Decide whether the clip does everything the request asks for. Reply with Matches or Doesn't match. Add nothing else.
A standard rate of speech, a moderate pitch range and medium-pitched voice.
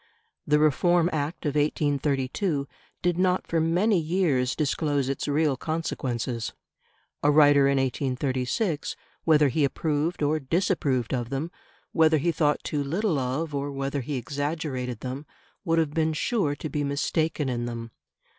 Matches